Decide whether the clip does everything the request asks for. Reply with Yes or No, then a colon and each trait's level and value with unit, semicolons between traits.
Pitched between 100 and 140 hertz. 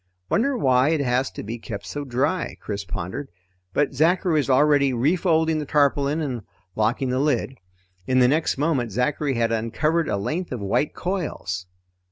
Yes: low, 135 Hz